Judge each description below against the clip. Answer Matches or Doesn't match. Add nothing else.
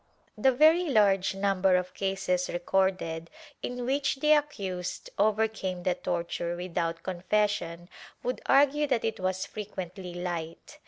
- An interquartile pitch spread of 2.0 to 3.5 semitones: Doesn't match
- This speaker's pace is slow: Matches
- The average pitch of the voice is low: Doesn't match